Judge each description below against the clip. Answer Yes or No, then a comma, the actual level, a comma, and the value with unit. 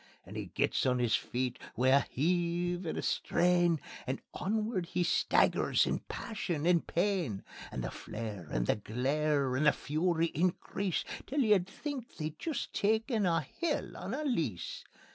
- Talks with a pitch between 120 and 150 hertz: No, medium, 170 Hz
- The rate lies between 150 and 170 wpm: Yes, average, 160 wpm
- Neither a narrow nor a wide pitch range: No, wide, 6.6 semitones